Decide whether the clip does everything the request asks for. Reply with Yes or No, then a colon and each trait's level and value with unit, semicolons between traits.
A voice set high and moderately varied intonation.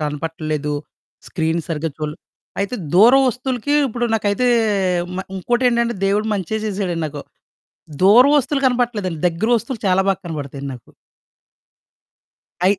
No: high, 195 Hz; wide, 6.7 semitones